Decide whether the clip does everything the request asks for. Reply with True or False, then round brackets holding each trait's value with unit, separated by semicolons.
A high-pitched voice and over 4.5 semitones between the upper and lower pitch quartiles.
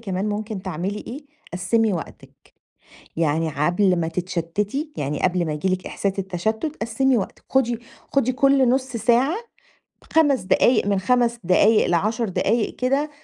True (210 Hz; 5.6 semitones)